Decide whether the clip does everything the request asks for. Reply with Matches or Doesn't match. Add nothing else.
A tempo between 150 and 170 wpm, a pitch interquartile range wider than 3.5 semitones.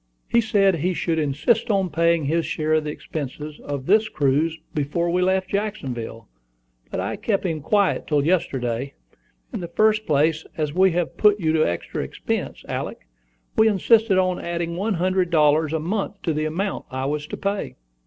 Doesn't match